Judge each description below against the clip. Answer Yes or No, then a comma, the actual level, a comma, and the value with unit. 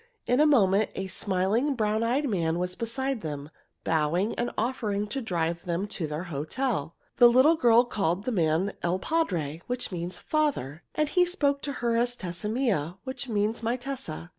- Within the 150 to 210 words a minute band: Yes, average, 180 wpm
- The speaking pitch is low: No, high, 210 Hz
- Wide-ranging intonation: Yes, wide, 6.7 semitones